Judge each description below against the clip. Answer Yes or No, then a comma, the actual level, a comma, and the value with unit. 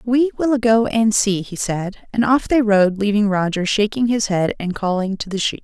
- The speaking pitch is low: No, high, 210 Hz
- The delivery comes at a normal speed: No, fast, 225 wpm